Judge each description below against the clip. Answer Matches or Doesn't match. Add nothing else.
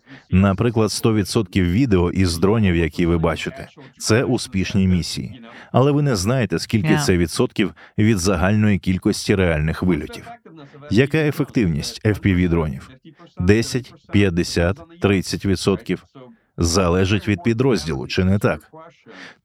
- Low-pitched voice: Matches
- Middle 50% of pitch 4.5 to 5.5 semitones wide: Matches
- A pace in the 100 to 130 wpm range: Matches